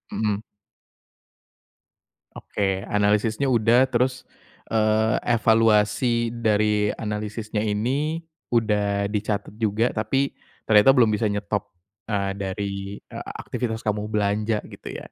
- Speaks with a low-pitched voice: Yes, low, 110 Hz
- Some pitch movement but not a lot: No, narrow, 1.8 semitones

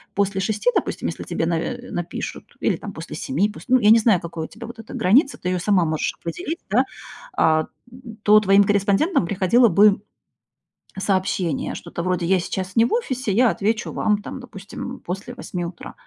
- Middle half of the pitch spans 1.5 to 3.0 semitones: No, average, 4.1 semitones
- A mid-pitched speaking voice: No, high, 200 Hz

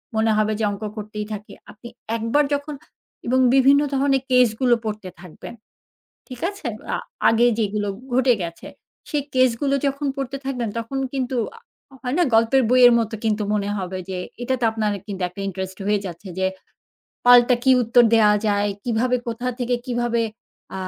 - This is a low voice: No, high, 235 Hz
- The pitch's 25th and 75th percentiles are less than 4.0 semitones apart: Yes, average, 3.6 semitones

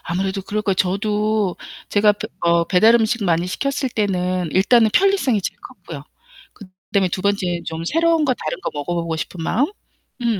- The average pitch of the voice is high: Yes, high, 200 Hz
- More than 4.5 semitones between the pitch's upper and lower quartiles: No, average, 3.6 semitones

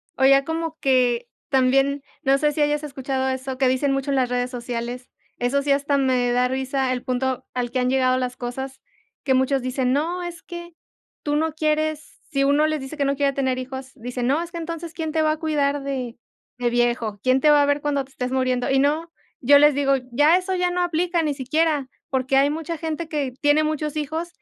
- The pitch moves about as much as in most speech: Yes, average, 3.0 semitones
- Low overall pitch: No, very high, 275 Hz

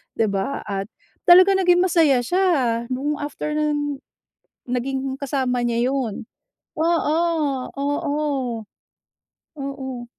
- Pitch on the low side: No, very high, 275 Hz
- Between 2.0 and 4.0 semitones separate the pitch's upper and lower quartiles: Yes, average, 3.4 semitones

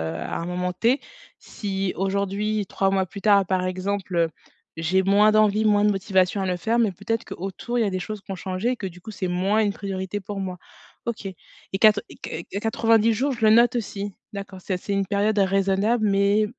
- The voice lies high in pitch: Yes, high, 200 Hz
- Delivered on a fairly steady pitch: Yes, narrow, 2.2 semitones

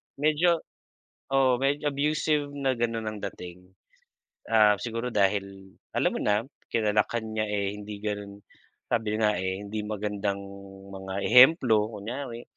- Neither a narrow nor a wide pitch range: Yes, average, 4.2 semitones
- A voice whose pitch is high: No, low, 110 Hz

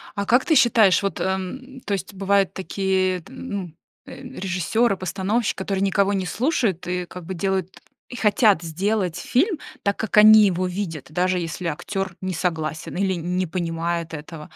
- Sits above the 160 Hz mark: Yes, high, 190 Hz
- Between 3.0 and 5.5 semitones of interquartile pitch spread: No, narrow, 2.5 semitones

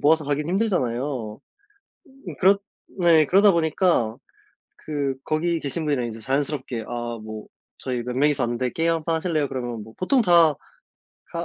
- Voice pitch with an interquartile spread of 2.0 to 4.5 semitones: No, wide, 5.6 semitones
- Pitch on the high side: No, medium, 150 Hz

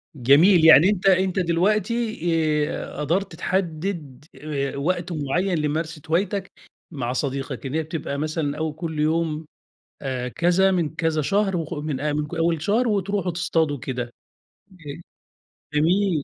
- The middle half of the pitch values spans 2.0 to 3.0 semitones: No, average, 3.8 semitones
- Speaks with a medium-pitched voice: Yes, medium, 165 Hz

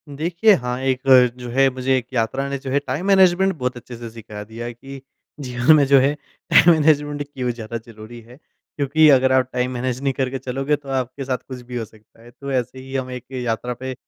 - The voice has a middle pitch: No, low, 130 Hz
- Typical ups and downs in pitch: No, narrow, 2.2 semitones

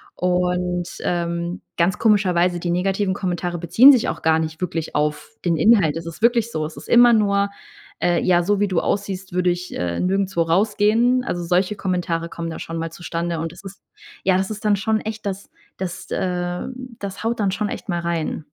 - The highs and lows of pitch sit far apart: No, average, 2.9 semitones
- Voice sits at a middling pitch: Yes, medium, 180 Hz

